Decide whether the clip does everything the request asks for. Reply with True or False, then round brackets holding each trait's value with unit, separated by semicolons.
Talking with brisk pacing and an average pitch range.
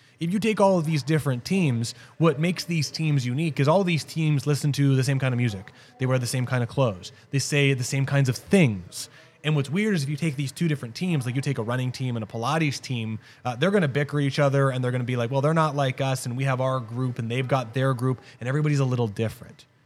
True (275 wpm; 3.3 semitones)